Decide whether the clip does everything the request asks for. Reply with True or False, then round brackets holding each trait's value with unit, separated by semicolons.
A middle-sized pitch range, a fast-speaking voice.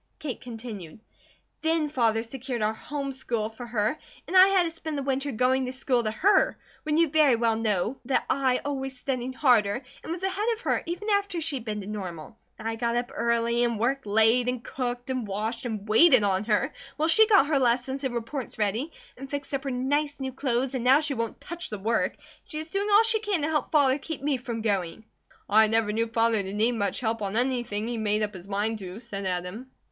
True (4.5 semitones; 225 wpm)